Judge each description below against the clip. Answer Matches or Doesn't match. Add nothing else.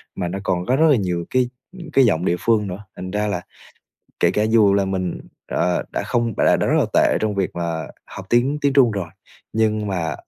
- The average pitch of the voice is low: Matches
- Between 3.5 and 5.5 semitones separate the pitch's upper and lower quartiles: Matches